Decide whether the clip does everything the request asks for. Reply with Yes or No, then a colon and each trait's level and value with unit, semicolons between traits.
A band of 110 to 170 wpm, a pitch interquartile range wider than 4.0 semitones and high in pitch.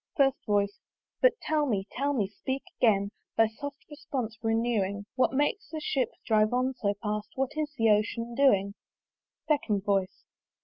Yes: average, 160 wpm; average, 5.0 semitones; high, 230 Hz